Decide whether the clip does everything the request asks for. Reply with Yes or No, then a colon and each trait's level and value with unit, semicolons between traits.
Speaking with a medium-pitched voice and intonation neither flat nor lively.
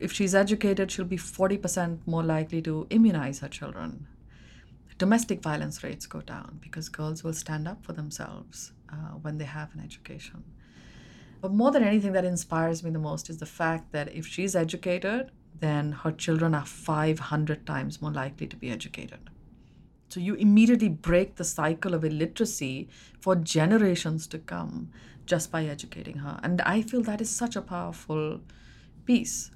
Yes: medium, 165 Hz; average, 3.7 semitones